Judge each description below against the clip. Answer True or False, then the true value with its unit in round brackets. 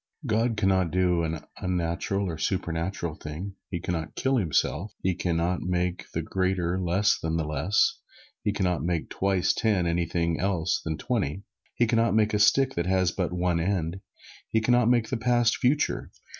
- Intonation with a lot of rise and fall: False (3.8 semitones)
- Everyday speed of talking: True (195 wpm)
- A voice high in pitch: False (90 Hz)